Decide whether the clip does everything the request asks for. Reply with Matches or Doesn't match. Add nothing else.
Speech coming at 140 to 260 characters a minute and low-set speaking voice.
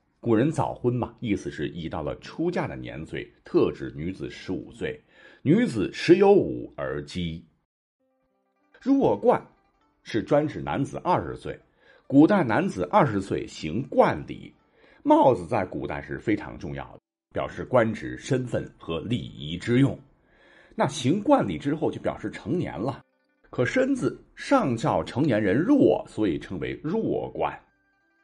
Matches